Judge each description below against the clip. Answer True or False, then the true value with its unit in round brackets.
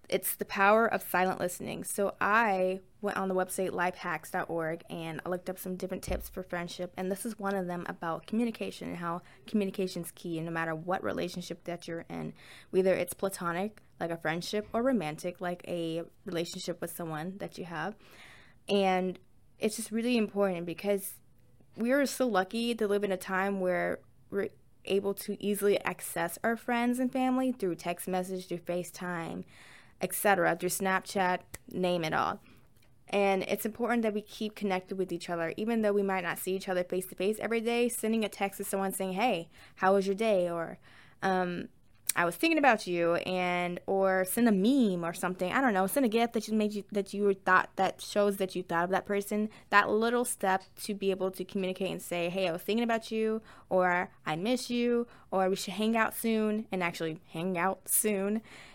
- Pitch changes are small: False (3.0 semitones)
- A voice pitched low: False (190 Hz)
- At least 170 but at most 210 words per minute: True (200 wpm)